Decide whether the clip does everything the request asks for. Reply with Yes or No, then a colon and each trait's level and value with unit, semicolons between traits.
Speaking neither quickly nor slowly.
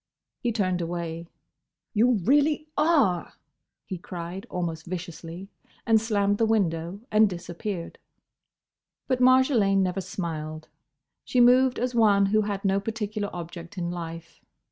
No: slow, 125 wpm